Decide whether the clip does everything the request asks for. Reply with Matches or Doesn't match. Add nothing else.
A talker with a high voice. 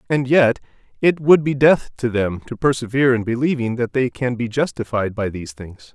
Doesn't match